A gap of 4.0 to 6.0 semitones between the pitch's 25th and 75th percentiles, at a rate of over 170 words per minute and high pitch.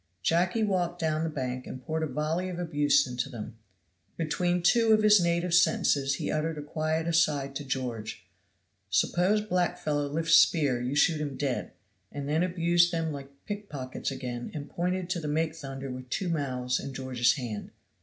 No: average, 4.3 semitones; average, 180 wpm; medium, 155 Hz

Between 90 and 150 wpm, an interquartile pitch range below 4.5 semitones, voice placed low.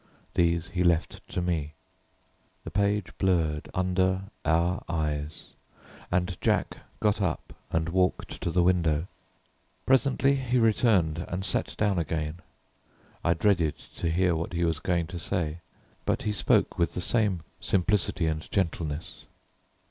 Yes: average, 140 wpm; average, 2.7 semitones; very low, 90 Hz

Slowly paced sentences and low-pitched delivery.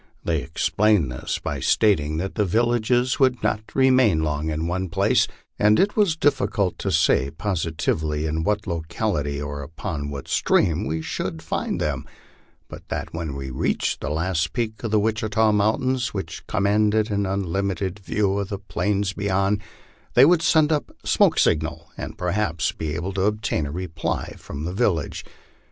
No: average, 170 wpm; very low, 95 Hz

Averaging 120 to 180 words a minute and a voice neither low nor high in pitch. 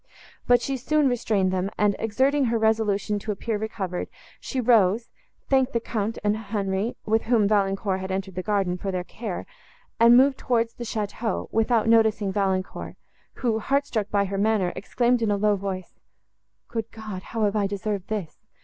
No: average, 175 wpm; high, 215 Hz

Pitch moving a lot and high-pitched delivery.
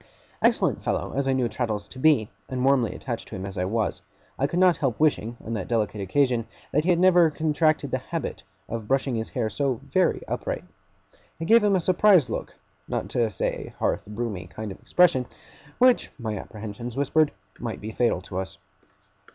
No: wide, 6.2 semitones; low, 125 Hz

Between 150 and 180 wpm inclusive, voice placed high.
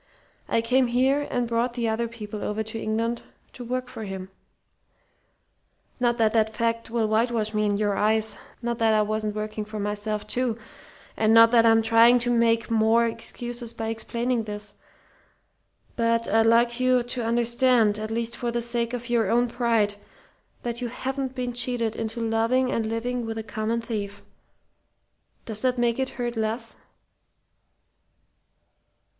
Yes: average, 160 wpm; high, 230 Hz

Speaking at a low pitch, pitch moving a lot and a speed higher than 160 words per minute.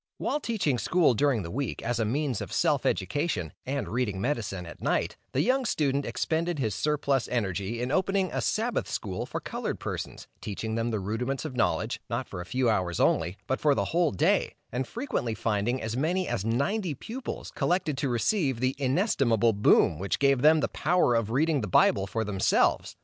Yes: low, 130 Hz; wide, 6.0 semitones; average, 195 wpm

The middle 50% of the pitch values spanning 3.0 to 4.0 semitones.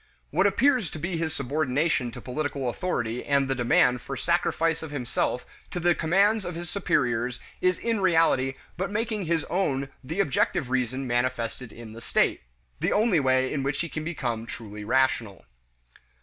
No: wide, 5.6 semitones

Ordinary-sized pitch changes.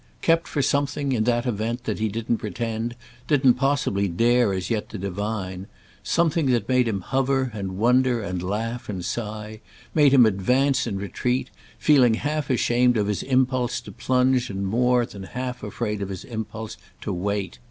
Yes: average, 3.9 semitones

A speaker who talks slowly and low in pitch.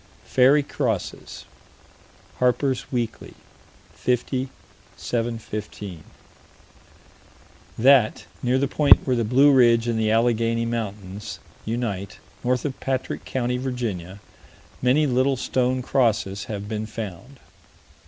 Yes: slow, 105 wpm; low, 120 Hz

